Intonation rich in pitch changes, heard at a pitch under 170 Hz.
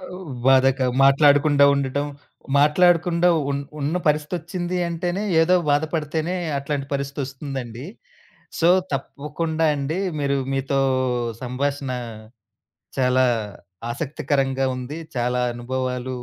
No: average, 3.2 semitones; medium, 140 Hz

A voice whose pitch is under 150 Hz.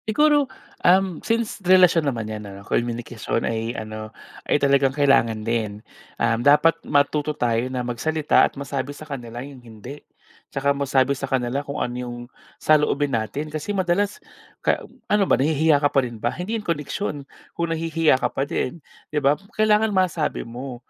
Yes: medium, 140 Hz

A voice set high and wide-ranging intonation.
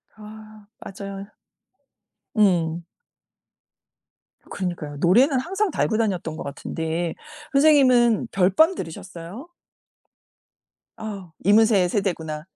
No: high, 200 Hz; average, 4.8 semitones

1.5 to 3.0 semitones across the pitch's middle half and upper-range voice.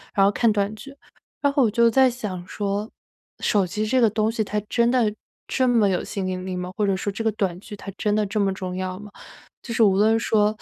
Yes: narrow, 2.5 semitones; high, 210 Hz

